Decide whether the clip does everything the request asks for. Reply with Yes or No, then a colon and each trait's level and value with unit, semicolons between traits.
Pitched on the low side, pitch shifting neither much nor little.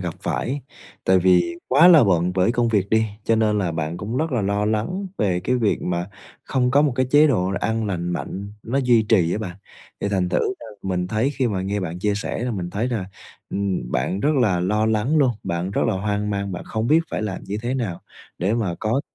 Yes: low, 105 Hz; average, 4.5 semitones